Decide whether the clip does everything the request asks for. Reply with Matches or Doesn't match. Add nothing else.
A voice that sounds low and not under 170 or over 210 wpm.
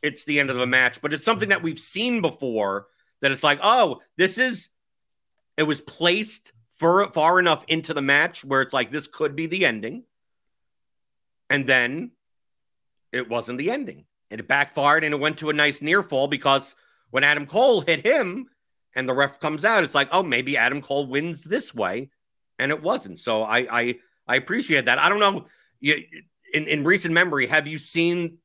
Doesn't match